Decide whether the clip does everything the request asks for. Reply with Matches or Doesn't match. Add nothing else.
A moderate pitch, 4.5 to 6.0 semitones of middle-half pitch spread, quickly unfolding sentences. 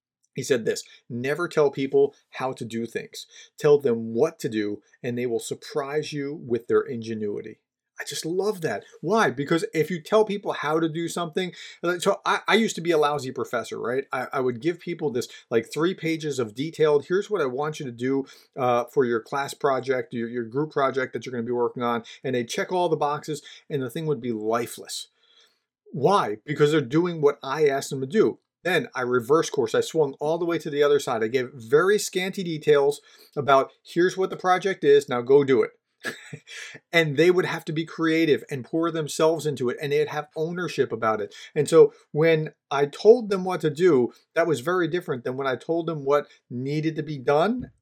Matches